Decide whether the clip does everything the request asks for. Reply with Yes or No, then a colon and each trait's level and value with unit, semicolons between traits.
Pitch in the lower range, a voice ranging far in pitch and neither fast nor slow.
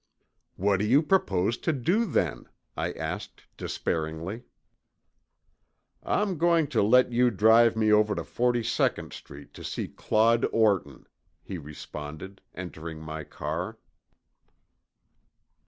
No: low, 105 Hz; wide, 6.6 semitones; slow, 120 wpm